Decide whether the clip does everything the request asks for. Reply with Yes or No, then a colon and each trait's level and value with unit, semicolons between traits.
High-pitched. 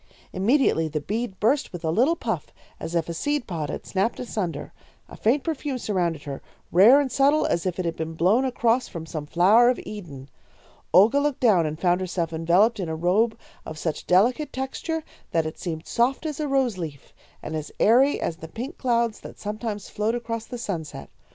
Yes: high, 210 Hz